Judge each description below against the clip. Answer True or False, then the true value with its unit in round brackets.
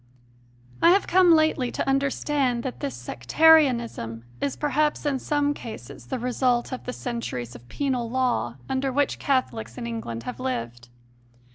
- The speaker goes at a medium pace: True (155 wpm)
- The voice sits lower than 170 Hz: False (250 Hz)